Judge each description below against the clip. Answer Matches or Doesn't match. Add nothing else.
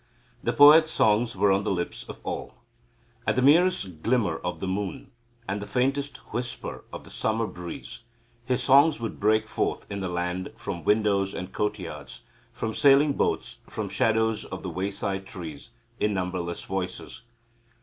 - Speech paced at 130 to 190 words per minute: Matches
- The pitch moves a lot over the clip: Doesn't match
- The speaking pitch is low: Matches